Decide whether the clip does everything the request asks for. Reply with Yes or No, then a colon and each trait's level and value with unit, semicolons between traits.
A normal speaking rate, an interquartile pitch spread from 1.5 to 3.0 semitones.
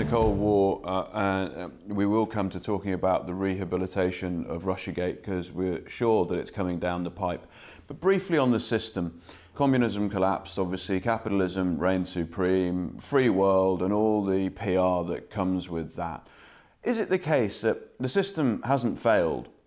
Yes: average, 170 wpm; narrow, 2.4 semitones